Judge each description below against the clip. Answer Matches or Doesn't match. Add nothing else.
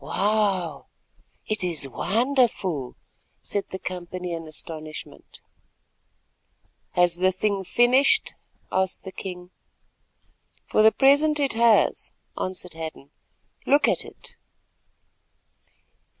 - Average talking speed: Doesn't match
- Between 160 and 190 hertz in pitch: Matches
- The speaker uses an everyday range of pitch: Matches